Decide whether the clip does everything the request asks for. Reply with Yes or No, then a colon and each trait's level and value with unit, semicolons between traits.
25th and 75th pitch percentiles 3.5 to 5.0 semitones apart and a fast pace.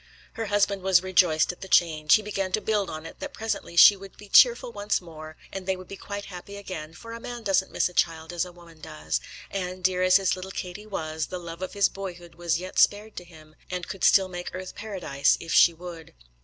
No: average, 2.8 semitones; fast, 235 wpm